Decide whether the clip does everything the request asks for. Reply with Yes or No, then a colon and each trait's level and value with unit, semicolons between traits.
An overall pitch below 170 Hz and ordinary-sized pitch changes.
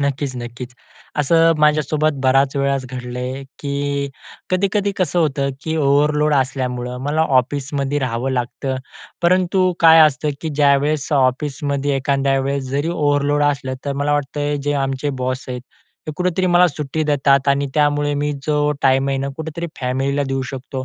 No: medium, 140 Hz; narrow, 2.0 semitones